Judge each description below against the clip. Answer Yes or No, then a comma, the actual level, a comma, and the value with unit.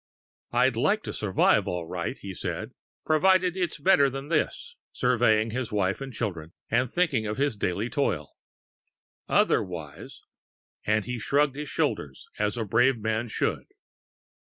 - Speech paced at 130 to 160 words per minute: Yes, average, 150 wpm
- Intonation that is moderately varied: No, wide, 5.7 semitones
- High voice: No, low, 115 Hz